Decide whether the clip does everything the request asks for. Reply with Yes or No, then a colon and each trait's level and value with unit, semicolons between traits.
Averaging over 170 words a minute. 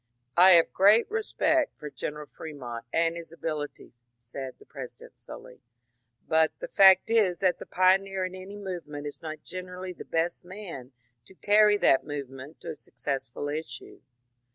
No: average, 165 wpm